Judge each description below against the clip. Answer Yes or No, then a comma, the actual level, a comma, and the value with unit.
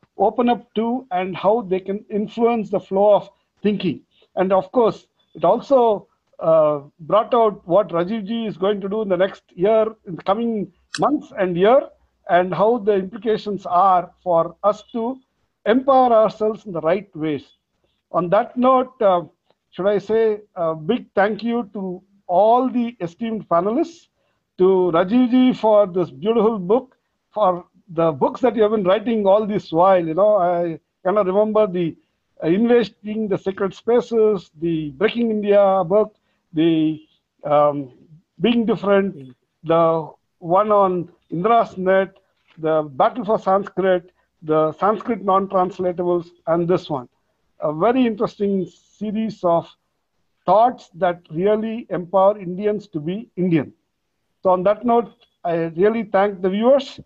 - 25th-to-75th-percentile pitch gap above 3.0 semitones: Yes, average, 3.9 semitones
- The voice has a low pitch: No, high, 195 Hz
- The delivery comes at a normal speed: Yes, average, 145 wpm